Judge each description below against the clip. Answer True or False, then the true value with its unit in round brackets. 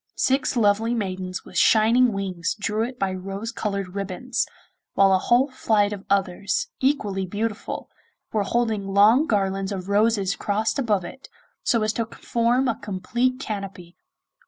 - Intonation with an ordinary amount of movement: True (3.0 semitones)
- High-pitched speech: True (205 Hz)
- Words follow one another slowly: False (150 wpm)